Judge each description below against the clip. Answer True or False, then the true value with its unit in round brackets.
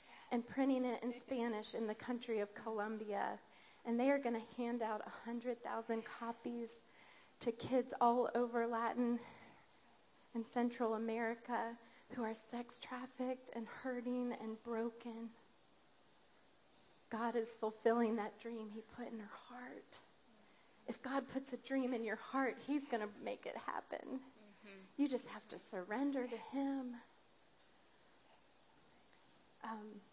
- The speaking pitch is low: False (235 Hz)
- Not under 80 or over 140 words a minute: True (135 wpm)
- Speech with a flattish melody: True (1.6 semitones)